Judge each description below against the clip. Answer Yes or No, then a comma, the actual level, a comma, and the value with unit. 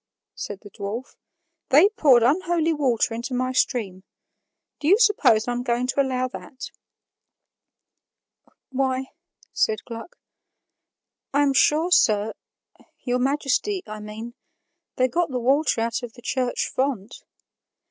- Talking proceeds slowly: Yes, slow, 125 wpm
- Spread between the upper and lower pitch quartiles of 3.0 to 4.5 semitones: Yes, average, 3.6 semitones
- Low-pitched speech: No, very high, 255 Hz